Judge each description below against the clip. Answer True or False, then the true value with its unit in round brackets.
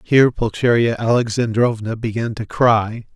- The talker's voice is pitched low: True (115 Hz)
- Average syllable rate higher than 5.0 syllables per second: False (4.7 syllables/s)